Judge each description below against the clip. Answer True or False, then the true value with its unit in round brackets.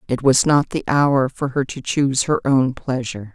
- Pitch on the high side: False (135 Hz)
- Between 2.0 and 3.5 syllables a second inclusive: False (4.9 syllables/s)